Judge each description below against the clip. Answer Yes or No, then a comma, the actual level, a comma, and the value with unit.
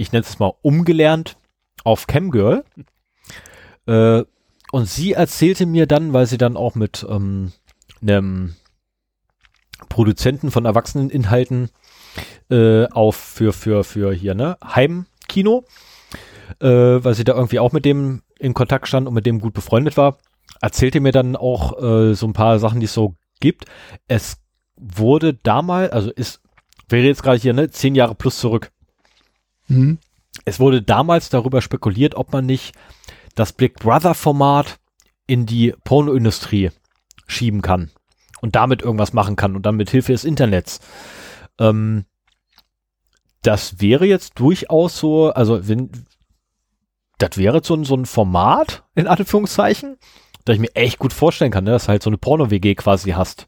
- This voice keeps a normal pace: Yes, average, 155 wpm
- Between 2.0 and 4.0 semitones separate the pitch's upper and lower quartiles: No, average, 4.6 semitones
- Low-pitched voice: Yes, low, 120 Hz